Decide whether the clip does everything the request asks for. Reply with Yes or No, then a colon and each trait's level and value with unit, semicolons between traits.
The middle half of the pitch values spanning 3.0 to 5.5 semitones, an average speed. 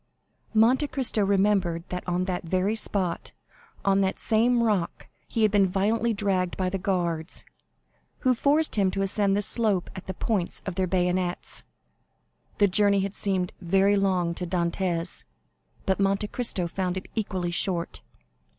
No: narrow, 2.5 semitones; average, 155 wpm